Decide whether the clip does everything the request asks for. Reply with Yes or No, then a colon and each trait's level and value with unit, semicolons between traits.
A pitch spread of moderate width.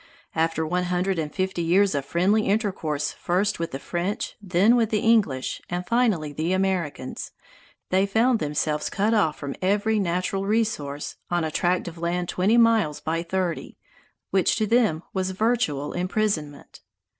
Yes: average, 4.3 semitones